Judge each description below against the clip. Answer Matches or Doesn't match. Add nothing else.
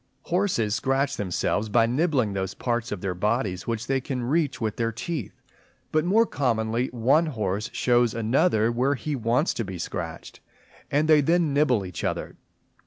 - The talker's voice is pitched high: Doesn't match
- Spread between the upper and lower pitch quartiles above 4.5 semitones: Matches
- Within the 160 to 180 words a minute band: Matches